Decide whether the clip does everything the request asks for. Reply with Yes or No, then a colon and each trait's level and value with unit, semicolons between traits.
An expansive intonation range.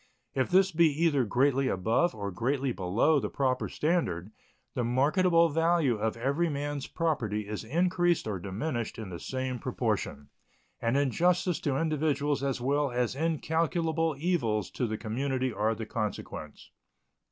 Yes: wide, 6.1 semitones